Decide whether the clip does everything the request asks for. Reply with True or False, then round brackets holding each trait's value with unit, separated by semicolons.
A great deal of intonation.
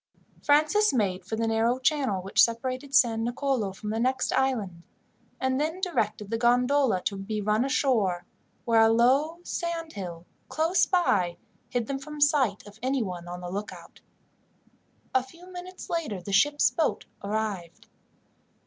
True (5.9 semitones)